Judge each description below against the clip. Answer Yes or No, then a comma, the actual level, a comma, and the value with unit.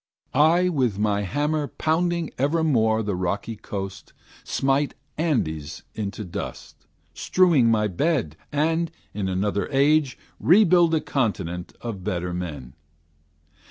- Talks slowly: Yes, slow, 115 wpm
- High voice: No, low, 115 Hz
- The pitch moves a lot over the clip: Yes, wide, 8.2 semitones